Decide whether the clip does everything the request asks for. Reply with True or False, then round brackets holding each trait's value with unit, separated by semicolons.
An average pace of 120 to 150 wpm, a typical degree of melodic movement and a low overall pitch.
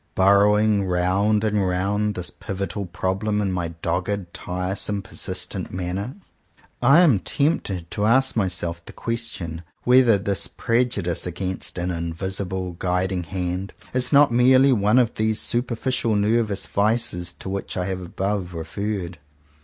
True (140 wpm; 3.2 semitones; 100 Hz)